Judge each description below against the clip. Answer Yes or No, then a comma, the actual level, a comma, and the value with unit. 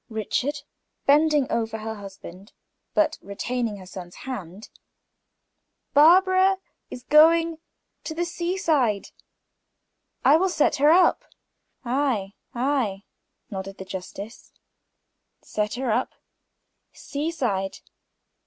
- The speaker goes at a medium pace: No, slow, 110 wpm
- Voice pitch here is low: No, very high, 250 Hz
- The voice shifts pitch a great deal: Yes, wide, 7.5 semitones